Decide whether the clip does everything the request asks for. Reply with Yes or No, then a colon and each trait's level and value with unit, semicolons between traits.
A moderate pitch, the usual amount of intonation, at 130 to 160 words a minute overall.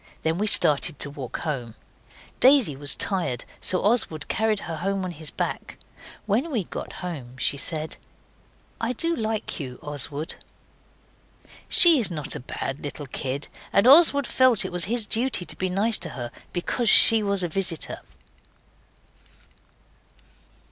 No: medium, 180 Hz; wide, 7.1 semitones; average, 150 wpm